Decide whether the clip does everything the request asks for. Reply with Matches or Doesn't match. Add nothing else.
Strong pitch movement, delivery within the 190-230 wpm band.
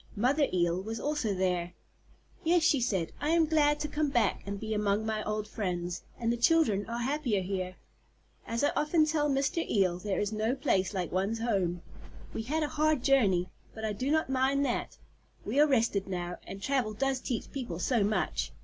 Matches